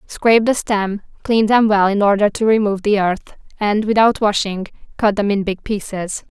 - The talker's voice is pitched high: Yes, high, 205 Hz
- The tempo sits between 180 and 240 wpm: Yes, average, 190 wpm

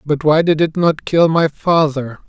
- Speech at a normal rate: No, fast, 210 wpm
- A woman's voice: No, male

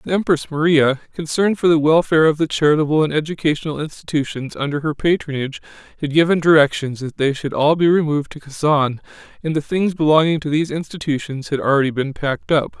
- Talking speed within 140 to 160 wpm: No, average, 185 wpm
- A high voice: No, medium, 150 Hz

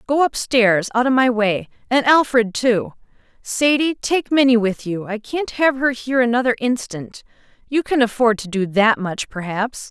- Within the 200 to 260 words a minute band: No, average, 180 wpm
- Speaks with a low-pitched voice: No, high, 235 Hz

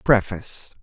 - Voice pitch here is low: Yes, low, 105 Hz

